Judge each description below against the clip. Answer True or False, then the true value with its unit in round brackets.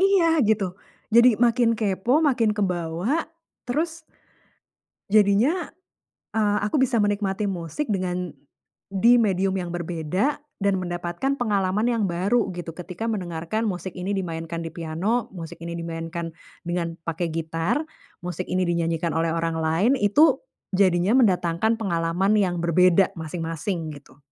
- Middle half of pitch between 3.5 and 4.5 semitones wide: True (4.1 semitones)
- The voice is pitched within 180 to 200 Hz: True (185 Hz)